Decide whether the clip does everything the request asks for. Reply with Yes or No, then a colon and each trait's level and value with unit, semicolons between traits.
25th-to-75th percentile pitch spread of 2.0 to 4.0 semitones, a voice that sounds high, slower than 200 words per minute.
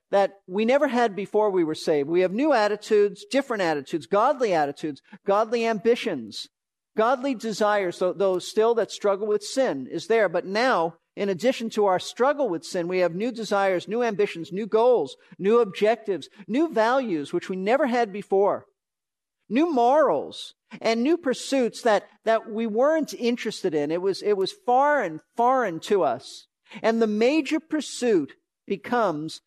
No: average, 4.6 semitones; high, 220 Hz; average, 160 wpm